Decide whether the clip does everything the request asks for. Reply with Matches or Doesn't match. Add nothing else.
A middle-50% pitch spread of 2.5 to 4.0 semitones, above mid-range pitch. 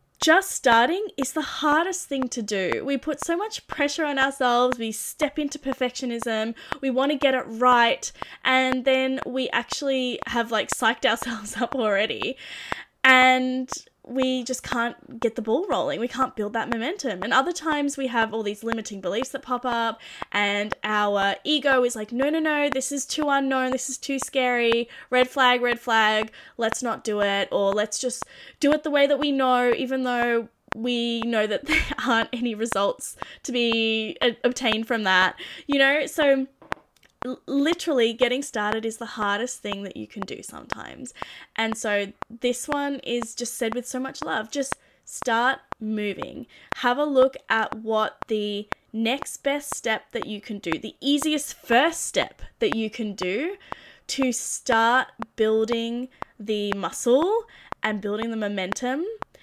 Matches